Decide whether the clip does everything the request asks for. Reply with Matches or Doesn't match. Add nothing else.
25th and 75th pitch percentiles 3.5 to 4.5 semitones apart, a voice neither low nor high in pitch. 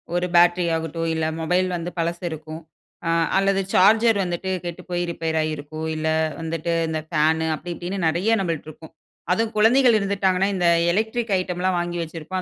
Doesn't match